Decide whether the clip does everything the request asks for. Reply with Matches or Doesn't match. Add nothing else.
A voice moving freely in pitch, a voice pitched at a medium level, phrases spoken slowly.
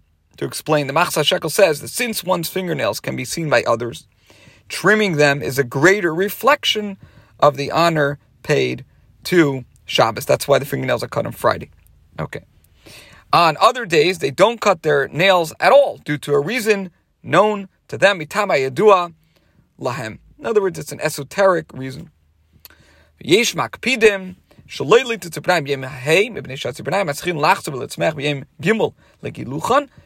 Matches